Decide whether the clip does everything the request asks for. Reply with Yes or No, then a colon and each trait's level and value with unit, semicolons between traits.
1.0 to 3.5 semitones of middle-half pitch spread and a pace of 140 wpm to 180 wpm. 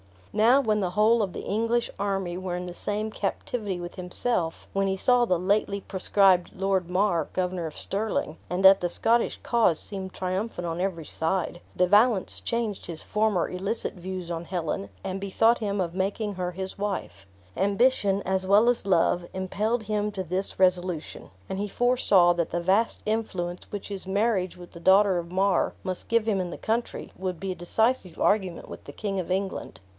No: average, 2.8 semitones; average, 190 wpm